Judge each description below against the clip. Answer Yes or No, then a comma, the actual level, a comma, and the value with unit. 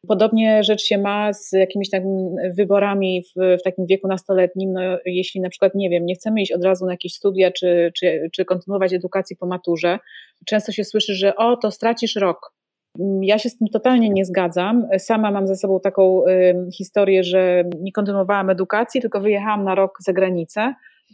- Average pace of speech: No, fast, 185 wpm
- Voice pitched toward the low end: No, high, 195 Hz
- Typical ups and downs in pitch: No, narrow, 2.3 semitones